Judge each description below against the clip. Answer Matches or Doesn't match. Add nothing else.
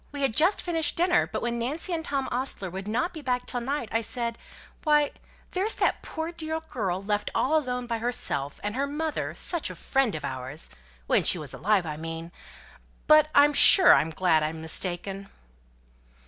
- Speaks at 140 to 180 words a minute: Doesn't match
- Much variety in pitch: Matches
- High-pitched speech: Matches